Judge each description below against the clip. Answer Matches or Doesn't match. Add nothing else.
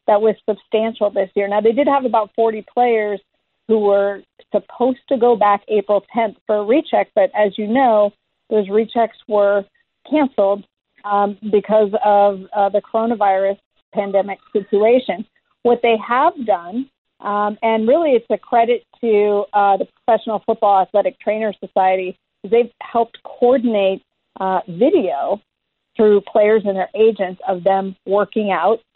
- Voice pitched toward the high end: Matches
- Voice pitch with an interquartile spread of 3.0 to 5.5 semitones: Doesn't match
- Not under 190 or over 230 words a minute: Doesn't match